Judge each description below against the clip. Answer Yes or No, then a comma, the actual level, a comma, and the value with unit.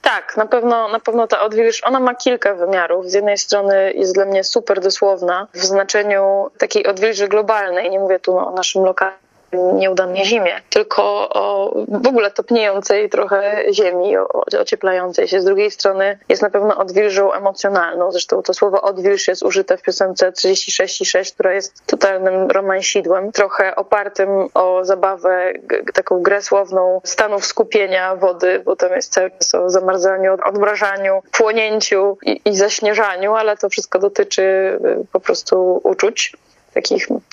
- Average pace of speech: Yes, average, 150 wpm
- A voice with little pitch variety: Yes, narrow, 2.3 semitones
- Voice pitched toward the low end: No, high, 200 Hz